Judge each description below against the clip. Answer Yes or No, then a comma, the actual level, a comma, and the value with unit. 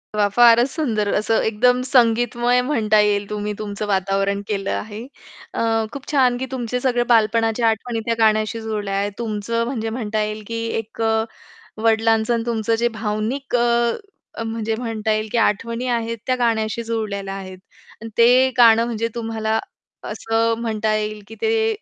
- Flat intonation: Yes, narrow, 1.8 semitones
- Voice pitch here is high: Yes, high, 225 Hz